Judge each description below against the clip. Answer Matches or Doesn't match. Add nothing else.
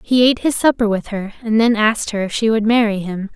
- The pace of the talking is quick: Matches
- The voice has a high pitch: Matches